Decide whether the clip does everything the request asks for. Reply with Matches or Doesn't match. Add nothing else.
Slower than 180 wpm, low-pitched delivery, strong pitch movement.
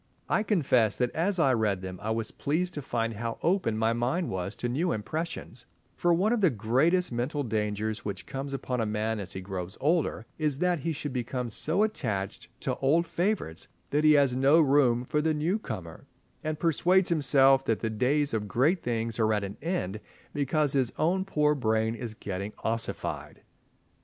Doesn't match